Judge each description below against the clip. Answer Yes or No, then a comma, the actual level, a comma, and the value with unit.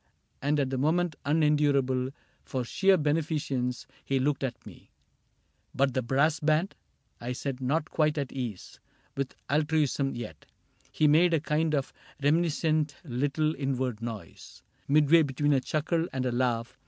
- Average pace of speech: Yes, average, 160 wpm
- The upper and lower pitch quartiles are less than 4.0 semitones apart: Yes, average, 3.1 semitones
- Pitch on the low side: No, medium, 145 Hz